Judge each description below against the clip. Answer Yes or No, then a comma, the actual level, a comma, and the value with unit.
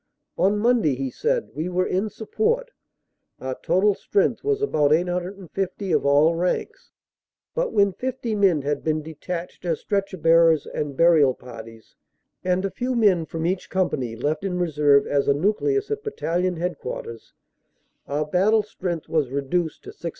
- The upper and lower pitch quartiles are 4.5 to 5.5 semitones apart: Yes, average, 5.2 semitones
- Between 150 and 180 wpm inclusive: Yes, average, 155 wpm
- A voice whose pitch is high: No, medium, 180 Hz